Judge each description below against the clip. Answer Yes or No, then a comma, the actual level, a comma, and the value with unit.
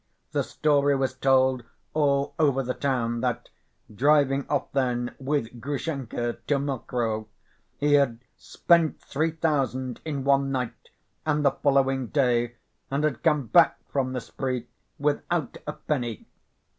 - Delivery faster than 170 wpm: No, slow, 135 wpm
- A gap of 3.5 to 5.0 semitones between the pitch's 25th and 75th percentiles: No, narrow, 2.6 semitones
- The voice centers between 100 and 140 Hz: Yes, low, 135 Hz